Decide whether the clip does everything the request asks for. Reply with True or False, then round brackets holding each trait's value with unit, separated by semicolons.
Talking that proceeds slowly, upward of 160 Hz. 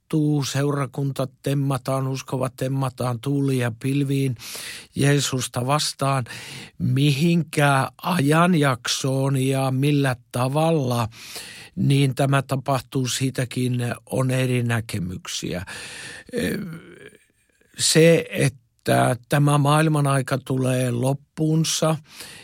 False (75 wpm; 135 Hz)